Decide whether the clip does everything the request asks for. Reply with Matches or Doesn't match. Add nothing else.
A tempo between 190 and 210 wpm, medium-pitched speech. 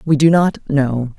Matches